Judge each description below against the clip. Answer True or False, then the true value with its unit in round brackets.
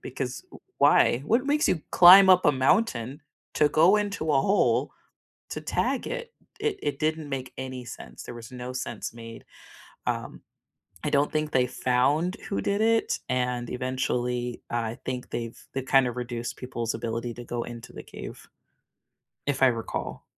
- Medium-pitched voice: False (130 Hz)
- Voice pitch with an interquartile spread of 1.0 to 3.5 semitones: False (4.6 semitones)